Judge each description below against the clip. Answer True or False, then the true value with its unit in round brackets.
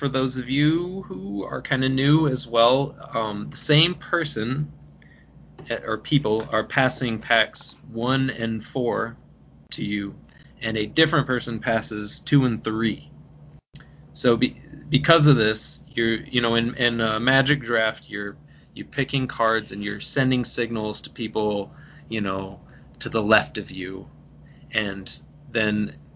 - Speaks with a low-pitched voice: True (115 Hz)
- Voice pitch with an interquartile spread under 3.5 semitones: False (4.4 semitones)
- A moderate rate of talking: True (155 wpm)